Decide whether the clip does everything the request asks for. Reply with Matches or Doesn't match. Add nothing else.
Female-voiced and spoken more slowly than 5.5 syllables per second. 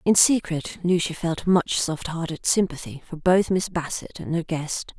Matches